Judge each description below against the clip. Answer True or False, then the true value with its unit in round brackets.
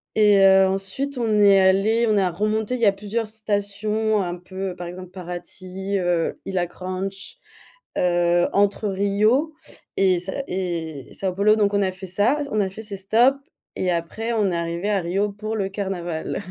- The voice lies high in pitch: True (195 Hz)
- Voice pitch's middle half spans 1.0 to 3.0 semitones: True (2.6 semitones)